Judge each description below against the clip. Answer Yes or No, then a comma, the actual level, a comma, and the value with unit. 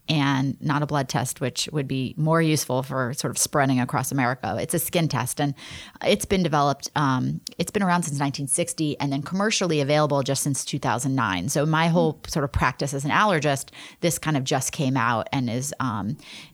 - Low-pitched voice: No, medium, 145 Hz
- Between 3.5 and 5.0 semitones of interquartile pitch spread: No, average, 2.9 semitones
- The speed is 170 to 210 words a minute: Yes, average, 200 wpm